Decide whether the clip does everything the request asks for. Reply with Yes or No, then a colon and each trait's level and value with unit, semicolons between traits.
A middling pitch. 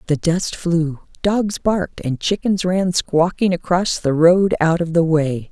Yes: medium, 170 Hz